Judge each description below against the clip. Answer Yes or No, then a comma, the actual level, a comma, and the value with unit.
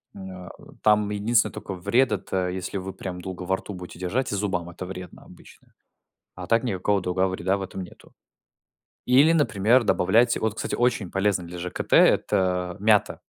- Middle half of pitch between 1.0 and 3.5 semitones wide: Yes, average, 2.8 semitones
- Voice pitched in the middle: No, very low, 95 Hz